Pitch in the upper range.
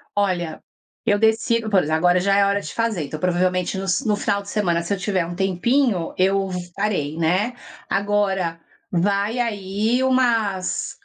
Yes: high, 195 Hz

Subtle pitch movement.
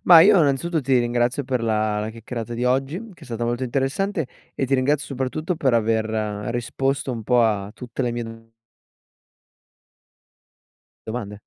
No: average, 3.1 semitones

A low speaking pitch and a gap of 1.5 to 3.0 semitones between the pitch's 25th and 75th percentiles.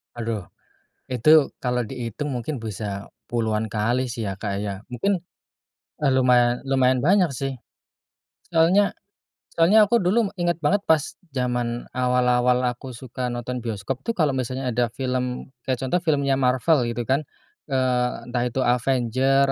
Yes: low, 125 Hz; narrow, 2.4 semitones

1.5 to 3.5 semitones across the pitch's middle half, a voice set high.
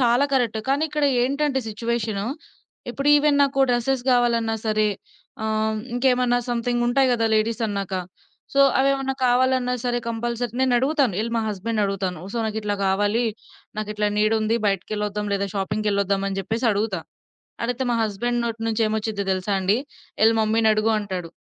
Yes: average, 2.8 semitones; high, 225 Hz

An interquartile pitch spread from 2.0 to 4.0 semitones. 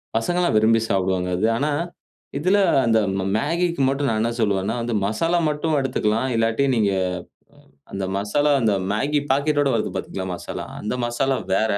No: wide, 5.4 semitones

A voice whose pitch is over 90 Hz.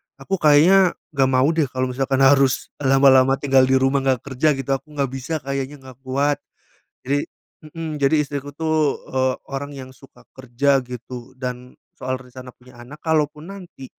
Yes: low, 135 Hz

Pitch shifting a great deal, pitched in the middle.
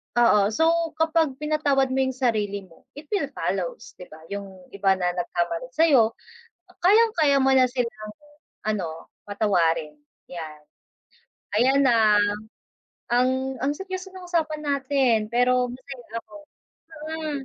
No: wide, 6.5 semitones; very high, 255 Hz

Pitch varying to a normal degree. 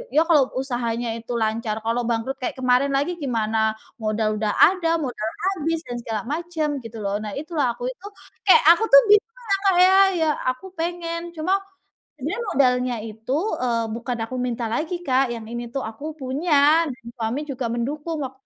No: wide, 5.8 semitones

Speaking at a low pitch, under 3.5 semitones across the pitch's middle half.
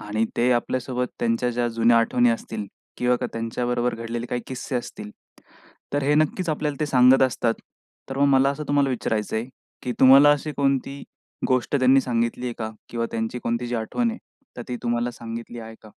Yes: low, 125 Hz; narrow, 2.6 semitones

